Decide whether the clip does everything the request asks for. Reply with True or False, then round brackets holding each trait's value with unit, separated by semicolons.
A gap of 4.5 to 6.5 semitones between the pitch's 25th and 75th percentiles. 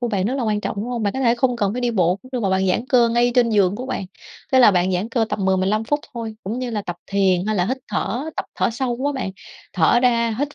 False (4.0 semitones)